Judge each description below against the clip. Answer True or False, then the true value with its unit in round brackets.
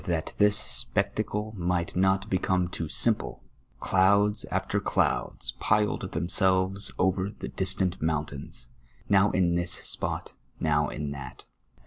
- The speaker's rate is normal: False (125 wpm)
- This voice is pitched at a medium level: False (95 Hz)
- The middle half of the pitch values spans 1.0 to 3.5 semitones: True (2.9 semitones)